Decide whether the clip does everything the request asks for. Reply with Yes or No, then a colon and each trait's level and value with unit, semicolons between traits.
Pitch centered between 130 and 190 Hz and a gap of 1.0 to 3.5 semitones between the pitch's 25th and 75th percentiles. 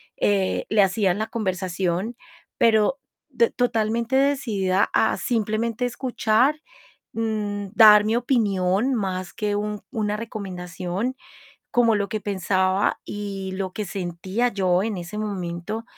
No: high, 210 Hz; average, 3.2 semitones